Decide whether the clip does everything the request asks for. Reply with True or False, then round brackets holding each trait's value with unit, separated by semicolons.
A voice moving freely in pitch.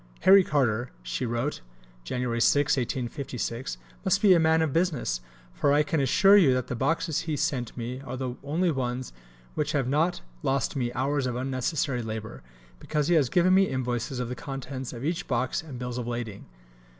False (4.0 semitones)